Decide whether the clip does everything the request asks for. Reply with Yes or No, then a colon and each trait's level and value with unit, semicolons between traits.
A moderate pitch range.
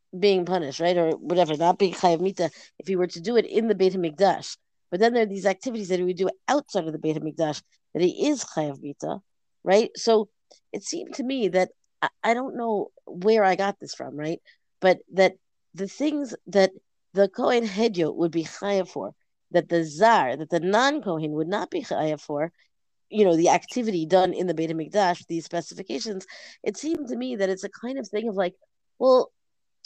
Yes: average, 4.6 semitones